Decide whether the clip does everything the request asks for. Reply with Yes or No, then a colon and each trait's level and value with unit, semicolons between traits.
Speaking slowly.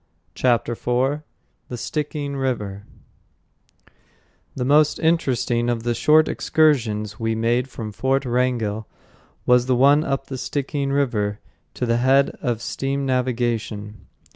Yes: slow, 125 wpm